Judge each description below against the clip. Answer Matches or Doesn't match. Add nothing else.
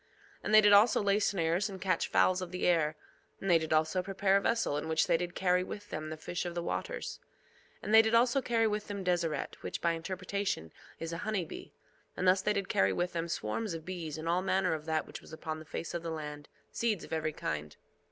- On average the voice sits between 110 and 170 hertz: Doesn't match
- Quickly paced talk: Matches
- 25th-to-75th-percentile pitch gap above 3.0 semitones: Matches